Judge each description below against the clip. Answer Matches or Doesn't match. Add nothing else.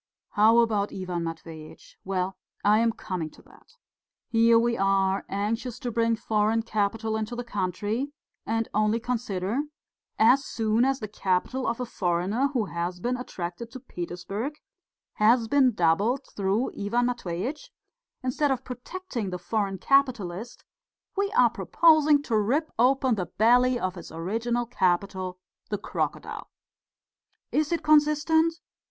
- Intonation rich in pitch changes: Doesn't match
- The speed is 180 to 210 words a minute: Doesn't match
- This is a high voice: Matches